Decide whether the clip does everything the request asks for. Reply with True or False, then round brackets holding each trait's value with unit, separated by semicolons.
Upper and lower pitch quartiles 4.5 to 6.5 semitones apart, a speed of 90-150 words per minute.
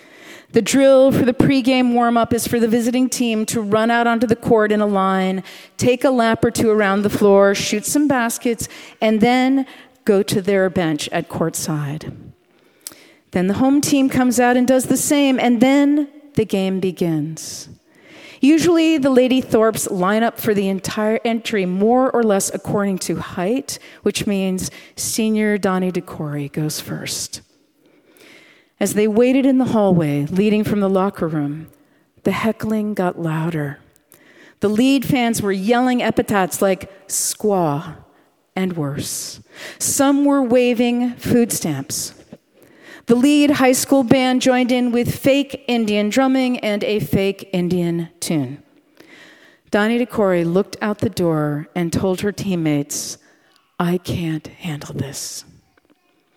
True (5.5 semitones; 145 wpm)